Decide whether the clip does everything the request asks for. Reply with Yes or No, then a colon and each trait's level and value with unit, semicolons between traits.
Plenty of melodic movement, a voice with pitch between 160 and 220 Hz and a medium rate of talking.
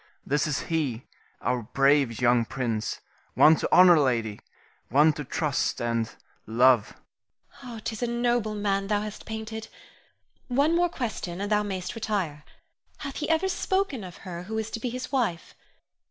Yes: wide, 8.7 semitones; medium, 185 Hz; average, 160 wpm